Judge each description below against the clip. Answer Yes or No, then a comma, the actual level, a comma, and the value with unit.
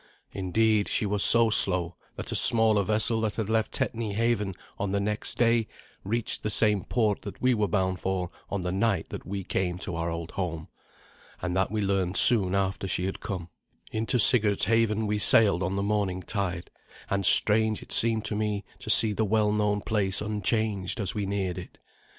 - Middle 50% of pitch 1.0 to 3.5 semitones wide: Yes, narrow, 2.6 semitones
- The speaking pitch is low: Yes, low, 100 Hz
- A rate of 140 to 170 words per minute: No, average, 190 wpm